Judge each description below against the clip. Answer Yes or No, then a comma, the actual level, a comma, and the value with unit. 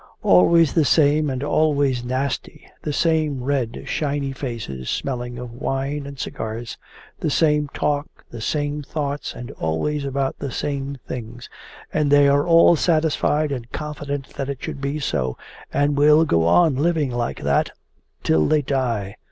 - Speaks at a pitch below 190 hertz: Yes, medium, 140 Hz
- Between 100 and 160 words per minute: Yes, average, 155 wpm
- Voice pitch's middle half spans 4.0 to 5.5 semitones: No, average, 3.3 semitones